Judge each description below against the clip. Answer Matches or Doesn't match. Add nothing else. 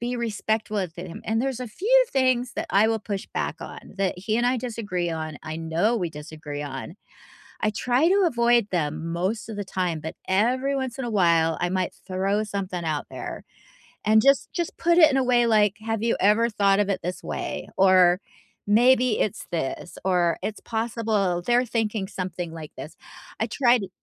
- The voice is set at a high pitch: Matches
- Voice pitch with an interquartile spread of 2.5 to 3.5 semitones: Doesn't match